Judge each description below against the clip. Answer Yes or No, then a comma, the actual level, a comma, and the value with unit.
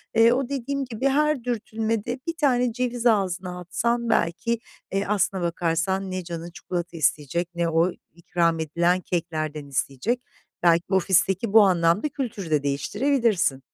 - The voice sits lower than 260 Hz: Yes, high, 190 Hz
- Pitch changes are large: Yes, wide, 5.8 semitones